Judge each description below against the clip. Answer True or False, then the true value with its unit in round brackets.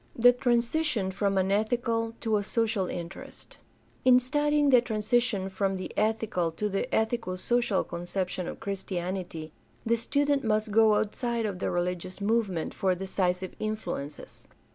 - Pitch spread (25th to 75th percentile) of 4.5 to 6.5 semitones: False (3.9 semitones)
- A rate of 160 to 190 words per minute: False (145 wpm)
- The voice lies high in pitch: True (210 Hz)